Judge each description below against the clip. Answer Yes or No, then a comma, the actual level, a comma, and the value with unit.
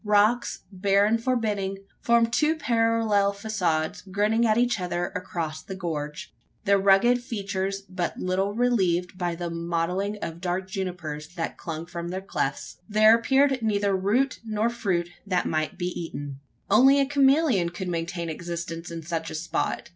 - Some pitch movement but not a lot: Yes, average, 4.4 semitones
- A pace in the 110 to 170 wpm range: Yes, average, 155 wpm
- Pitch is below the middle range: No, high, 195 Hz